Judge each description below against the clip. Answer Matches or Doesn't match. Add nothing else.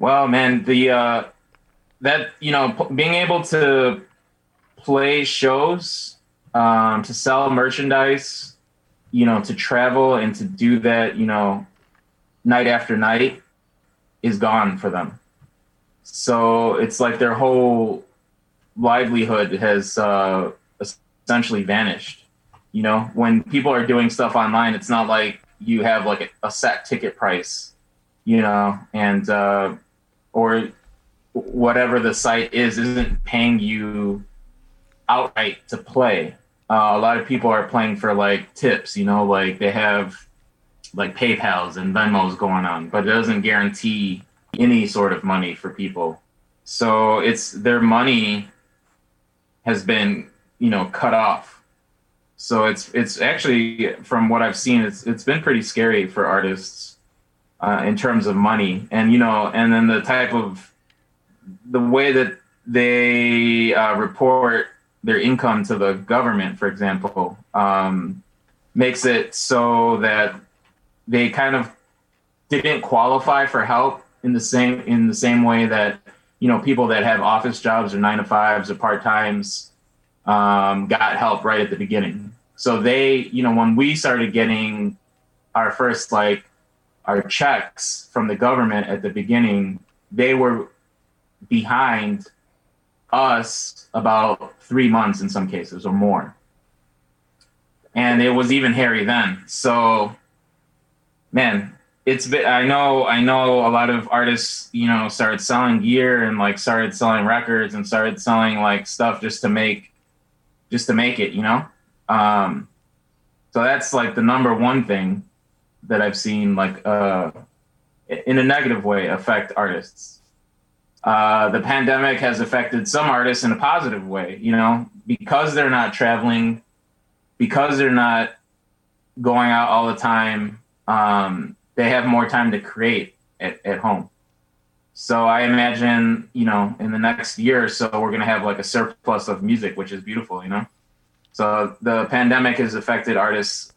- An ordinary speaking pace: Matches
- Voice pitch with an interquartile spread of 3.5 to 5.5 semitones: Matches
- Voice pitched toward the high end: Doesn't match